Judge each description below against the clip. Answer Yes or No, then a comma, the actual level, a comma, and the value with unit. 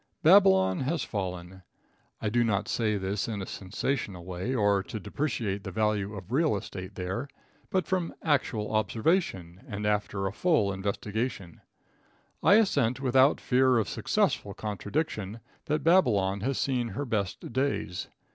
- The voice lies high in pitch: No, low, 105 Hz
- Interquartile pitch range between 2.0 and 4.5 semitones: No, average, 5.3 semitones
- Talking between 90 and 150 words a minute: Yes, average, 145 wpm